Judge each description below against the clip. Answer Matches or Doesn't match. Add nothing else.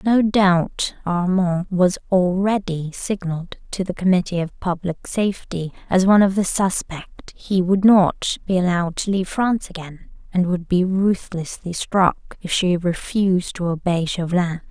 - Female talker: Matches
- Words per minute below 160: Matches